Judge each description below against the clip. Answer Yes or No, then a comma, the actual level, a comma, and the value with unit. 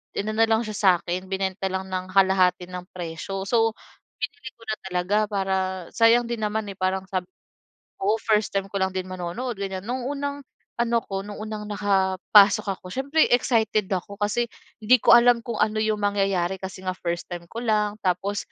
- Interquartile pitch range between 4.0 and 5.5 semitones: No, average, 2.8 semitones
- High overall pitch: Yes, high, 200 Hz